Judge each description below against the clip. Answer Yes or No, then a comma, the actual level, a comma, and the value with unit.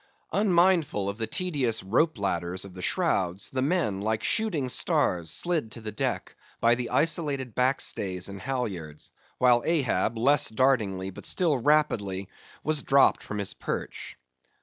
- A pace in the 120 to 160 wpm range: Yes, average, 150 wpm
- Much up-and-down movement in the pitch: Yes, wide, 7.3 semitones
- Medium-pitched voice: No, low, 120 Hz